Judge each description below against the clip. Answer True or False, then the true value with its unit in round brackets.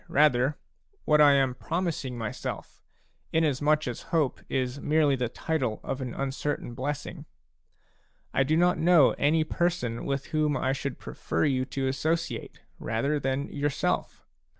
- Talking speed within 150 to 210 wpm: False (140 wpm)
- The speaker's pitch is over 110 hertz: True (140 Hz)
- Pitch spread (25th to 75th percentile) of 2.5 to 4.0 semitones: True (2.8 semitones)